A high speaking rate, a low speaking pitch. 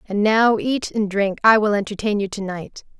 No: fast, 220 wpm; high, 210 Hz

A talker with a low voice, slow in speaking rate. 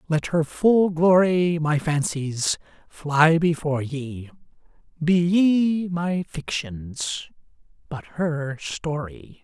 No: medium, 160 Hz; slow, 95 wpm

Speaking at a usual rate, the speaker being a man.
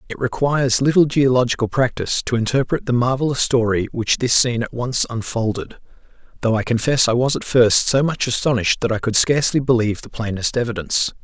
Yes: average, 180 wpm; male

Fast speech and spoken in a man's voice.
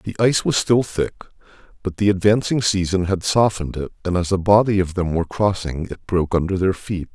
Yes: fast, 210 wpm; male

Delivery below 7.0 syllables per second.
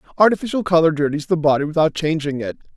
No: 7.2 syllables/s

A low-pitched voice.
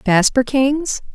No: very high, 255 Hz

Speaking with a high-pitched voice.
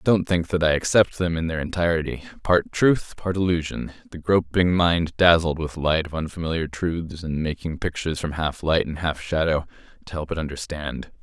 No: very low, 80 Hz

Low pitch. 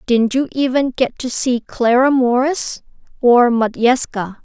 No: very high, 250 Hz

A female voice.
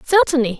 Yes: female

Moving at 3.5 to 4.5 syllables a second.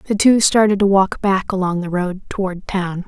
No: 4.7 syllables/s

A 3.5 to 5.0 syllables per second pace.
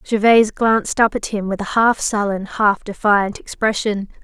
Yes: 4.9 syllables/s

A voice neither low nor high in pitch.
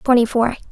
No: high, 240 Hz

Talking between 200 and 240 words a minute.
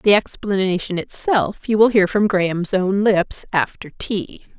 No: average, 145 wpm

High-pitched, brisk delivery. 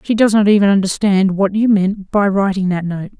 Yes: high, 200 Hz; fast, 225 wpm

